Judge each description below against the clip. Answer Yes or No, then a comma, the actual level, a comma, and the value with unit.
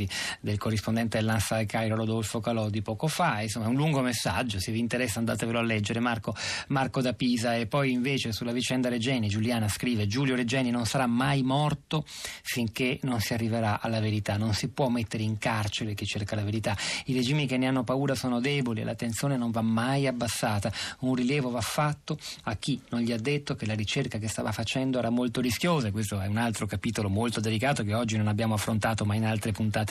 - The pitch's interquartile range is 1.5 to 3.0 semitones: Yes, average, 2.7 semitones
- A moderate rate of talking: No, fast, 210 wpm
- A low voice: Yes, low, 120 Hz